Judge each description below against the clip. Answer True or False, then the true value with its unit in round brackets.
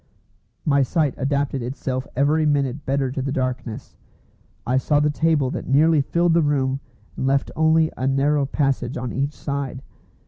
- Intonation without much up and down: True (2.1 semitones)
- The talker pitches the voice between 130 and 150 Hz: True (140 Hz)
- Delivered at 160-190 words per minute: True (165 wpm)